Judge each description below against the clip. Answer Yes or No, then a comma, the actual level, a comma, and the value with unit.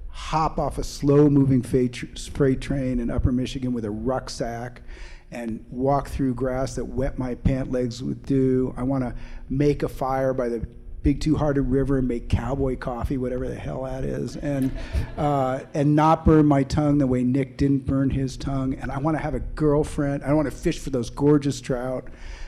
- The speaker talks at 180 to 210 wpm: Yes, average, 195 wpm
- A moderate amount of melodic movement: No, narrow, 2.1 semitones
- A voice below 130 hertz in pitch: No, low, 135 Hz